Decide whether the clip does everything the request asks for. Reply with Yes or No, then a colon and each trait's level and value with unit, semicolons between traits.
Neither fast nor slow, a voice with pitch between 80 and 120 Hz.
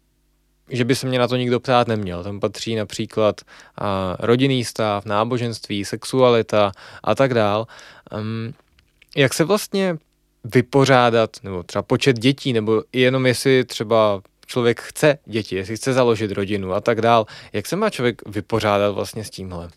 Yes: average, 150 wpm; low, 115 Hz